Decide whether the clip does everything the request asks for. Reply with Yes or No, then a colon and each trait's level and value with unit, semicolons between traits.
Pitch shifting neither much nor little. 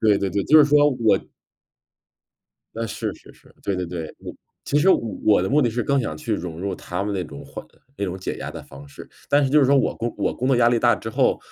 No: wide, 6.0 semitones